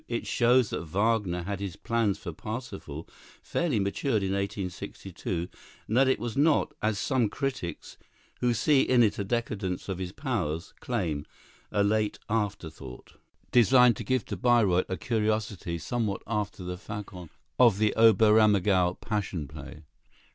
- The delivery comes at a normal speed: Yes, average, 145 wpm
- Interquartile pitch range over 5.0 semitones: No, average, 4.2 semitones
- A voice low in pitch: Yes, low, 105 Hz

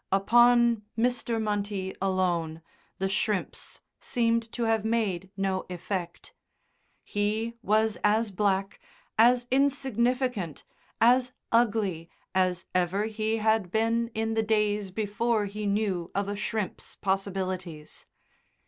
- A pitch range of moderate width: Yes, average, 3.1 semitones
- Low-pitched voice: No, high, 210 Hz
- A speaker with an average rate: No, slow, 110 wpm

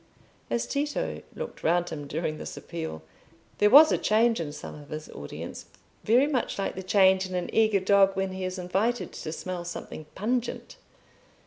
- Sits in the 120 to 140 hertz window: No, high, 190 Hz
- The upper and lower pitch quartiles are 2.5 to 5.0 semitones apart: Yes, average, 4.7 semitones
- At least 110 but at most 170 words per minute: No, average, 180 wpm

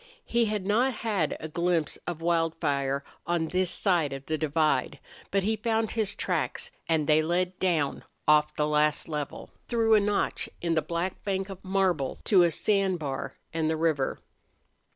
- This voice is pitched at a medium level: Yes, medium, 170 Hz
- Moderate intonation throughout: Yes, average, 4.4 semitones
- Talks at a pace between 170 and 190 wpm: Yes, average, 175 wpm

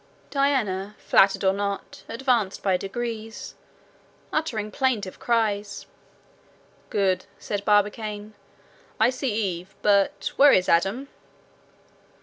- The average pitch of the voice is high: Yes, high, 210 Hz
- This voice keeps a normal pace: No, slow, 100 wpm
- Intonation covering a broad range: No, average, 3.2 semitones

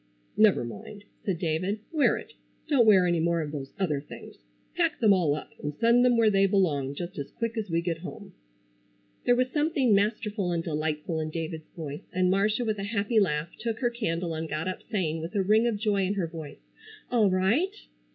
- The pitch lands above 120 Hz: Yes, high, 190 Hz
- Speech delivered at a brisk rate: Yes, fast, 210 wpm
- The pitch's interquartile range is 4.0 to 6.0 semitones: Yes, average, 5.1 semitones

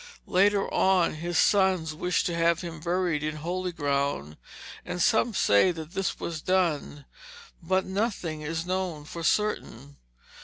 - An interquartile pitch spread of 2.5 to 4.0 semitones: Yes, average, 3.3 semitones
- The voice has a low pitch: No, medium, 170 Hz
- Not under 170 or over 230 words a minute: No, average, 145 wpm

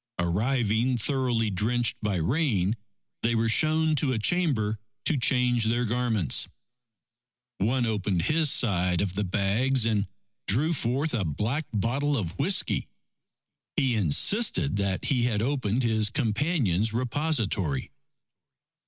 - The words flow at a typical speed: No, slow, 125 wpm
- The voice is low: Yes, low, 115 Hz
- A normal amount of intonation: Yes, average, 4.6 semitones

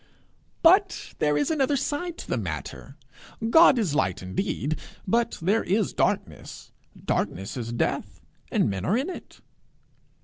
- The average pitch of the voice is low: No, high, 205 Hz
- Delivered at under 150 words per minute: Yes, average, 140 wpm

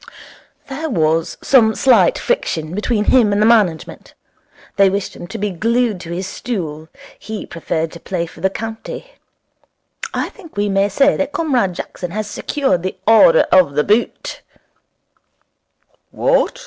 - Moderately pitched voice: No, high, 205 Hz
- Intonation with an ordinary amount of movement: No, wide, 5.8 semitones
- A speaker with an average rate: Yes, average, 150 wpm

